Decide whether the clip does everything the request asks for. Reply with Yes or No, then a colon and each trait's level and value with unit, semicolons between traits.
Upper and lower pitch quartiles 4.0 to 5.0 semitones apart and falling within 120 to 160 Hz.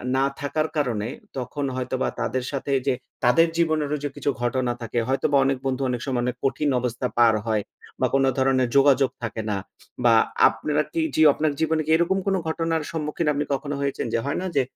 No: average, 3.4 semitones; medium, 140 Hz